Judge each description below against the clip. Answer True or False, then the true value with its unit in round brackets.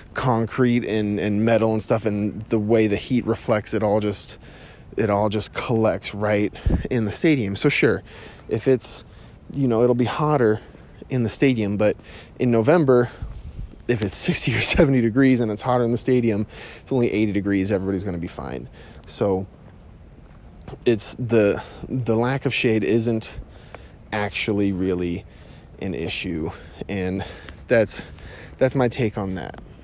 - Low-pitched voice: True (110 Hz)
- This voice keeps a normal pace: True (155 wpm)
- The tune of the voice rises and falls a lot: False (3.2 semitones)